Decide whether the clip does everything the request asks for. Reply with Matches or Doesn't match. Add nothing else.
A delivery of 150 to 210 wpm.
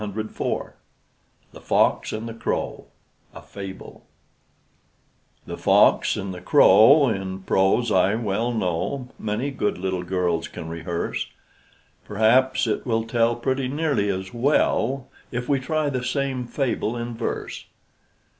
Doesn't match